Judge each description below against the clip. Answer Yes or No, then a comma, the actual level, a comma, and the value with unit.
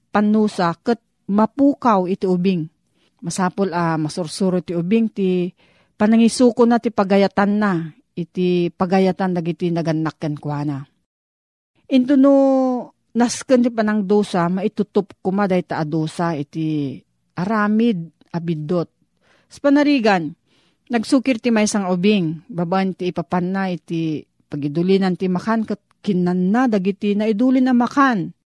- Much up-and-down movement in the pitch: No, average, 4.4 semitones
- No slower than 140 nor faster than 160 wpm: No, average, 130 wpm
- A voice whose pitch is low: No, high, 190 Hz